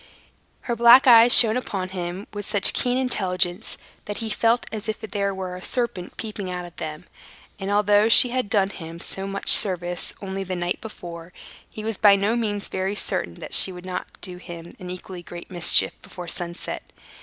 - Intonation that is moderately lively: Yes, average, 3.4 semitones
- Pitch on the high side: Yes, high, 195 Hz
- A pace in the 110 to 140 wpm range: No, average, 195 wpm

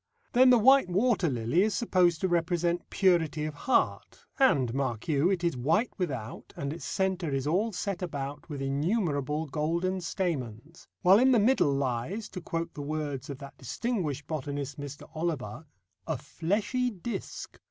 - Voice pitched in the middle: Yes, medium, 165 Hz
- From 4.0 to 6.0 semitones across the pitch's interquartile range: Yes, average, 5.2 semitones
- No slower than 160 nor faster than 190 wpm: Yes, average, 165 wpm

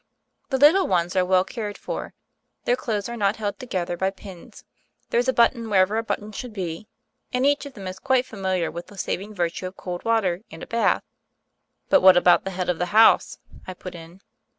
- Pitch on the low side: No, high, 195 Hz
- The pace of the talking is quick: Yes, fast, 210 wpm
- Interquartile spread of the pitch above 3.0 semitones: Yes, average, 4.2 semitones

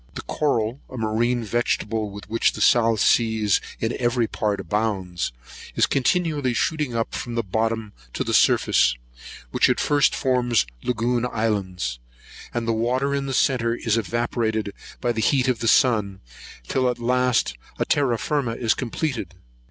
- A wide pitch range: No, narrow, 2.5 semitones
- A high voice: No, low, 115 Hz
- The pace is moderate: Yes, average, 160 wpm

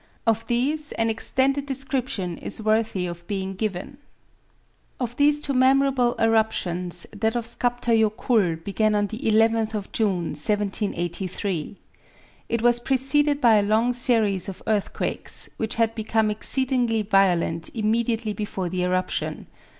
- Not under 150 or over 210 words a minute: No, slow, 135 wpm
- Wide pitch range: No, average, 3.7 semitones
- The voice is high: Yes, high, 220 Hz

